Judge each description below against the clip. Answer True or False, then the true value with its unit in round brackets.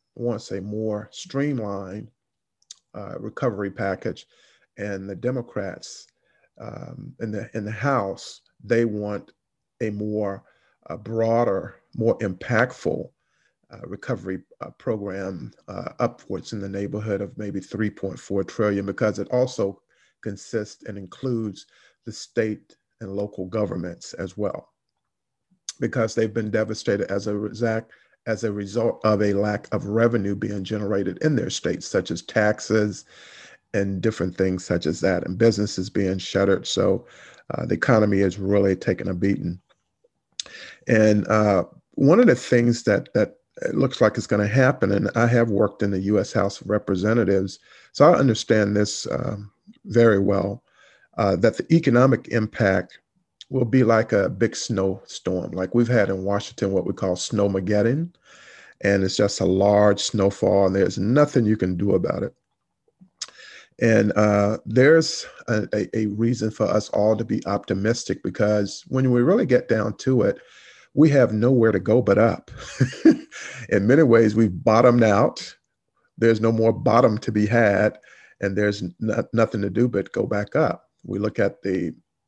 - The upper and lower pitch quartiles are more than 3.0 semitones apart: False (2.7 semitones)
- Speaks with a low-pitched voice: True (105 Hz)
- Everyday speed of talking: True (155 wpm)